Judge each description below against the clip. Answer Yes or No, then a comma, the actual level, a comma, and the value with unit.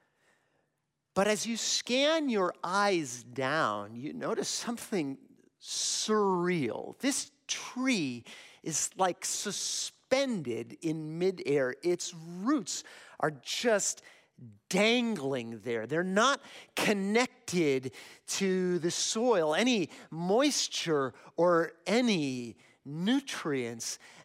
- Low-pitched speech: No, medium, 185 Hz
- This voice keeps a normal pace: No, slow, 85 wpm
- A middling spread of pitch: No, wide, 8.0 semitones